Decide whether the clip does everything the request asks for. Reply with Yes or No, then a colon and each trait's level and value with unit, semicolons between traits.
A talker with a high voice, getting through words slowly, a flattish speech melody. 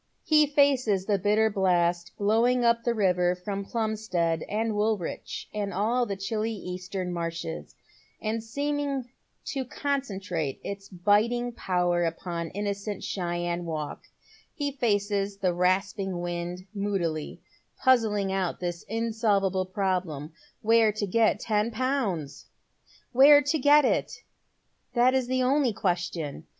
No: high, 205 Hz; slow, 125 wpm; average, 4.4 semitones